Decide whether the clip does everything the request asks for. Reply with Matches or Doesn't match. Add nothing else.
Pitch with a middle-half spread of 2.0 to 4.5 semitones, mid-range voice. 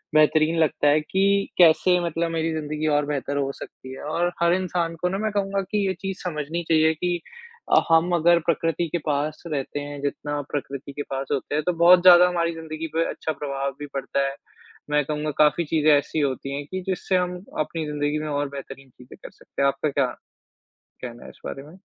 Matches